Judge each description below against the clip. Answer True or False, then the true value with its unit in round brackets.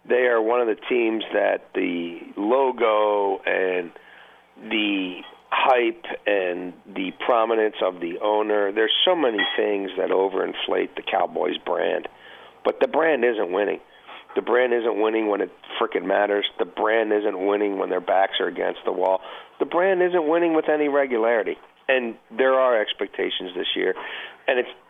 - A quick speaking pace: False (160 wpm)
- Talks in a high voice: False (130 Hz)